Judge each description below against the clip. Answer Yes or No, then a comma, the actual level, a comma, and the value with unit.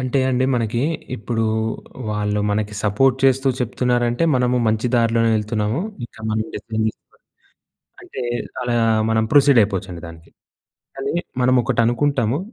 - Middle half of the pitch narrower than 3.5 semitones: Yes, average, 2.9 semitones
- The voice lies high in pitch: No, low, 115 Hz